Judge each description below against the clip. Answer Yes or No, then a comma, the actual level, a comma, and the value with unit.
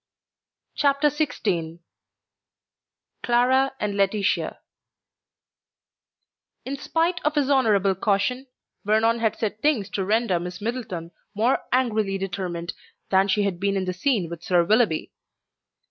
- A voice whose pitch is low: No, high, 210 Hz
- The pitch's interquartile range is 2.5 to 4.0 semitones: No, average, 5.0 semitones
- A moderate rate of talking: No, slow, 120 wpm